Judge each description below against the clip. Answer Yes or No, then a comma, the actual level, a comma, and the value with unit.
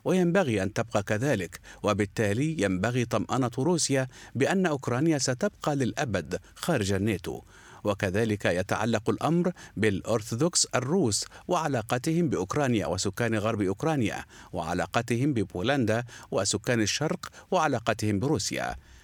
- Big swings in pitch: Yes, wide, 5.7 semitones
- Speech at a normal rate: Yes, average, 95 wpm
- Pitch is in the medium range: No, low, 115 Hz